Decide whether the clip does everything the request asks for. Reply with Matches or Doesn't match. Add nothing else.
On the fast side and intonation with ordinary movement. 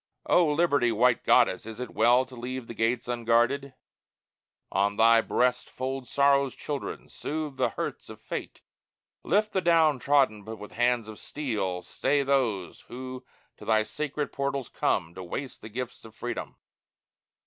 Doesn't match